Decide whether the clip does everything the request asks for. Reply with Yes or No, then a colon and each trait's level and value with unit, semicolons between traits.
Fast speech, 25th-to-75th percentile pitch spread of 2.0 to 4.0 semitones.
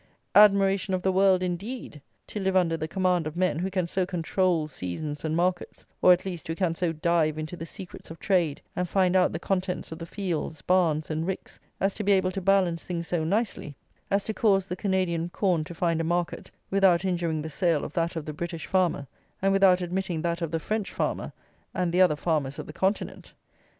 Yes: fast, 215 wpm; narrow, 2.6 semitones